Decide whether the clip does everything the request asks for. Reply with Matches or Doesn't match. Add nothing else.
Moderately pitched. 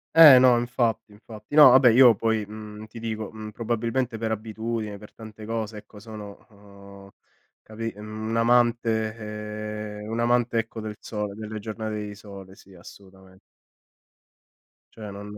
Doesn't match